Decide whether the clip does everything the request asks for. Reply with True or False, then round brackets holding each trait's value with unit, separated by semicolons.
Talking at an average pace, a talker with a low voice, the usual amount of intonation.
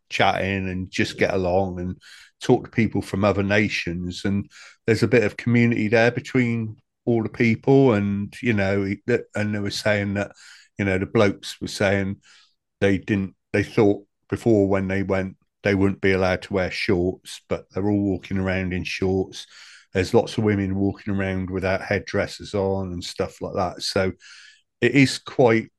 False (175 wpm; 100 Hz; 2.0 semitones)